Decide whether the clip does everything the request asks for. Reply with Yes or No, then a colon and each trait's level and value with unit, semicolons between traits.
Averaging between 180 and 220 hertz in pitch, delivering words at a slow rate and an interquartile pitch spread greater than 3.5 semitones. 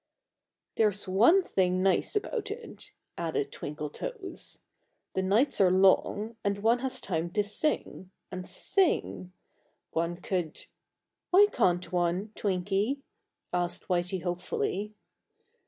Yes: high, 190 Hz; slow, 115 wpm; average, 4.2 semitones